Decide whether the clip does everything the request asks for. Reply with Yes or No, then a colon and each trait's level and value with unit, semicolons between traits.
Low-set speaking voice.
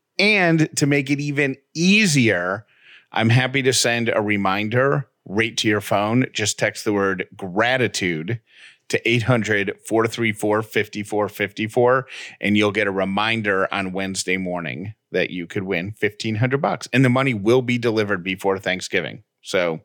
Yes: low, 110 Hz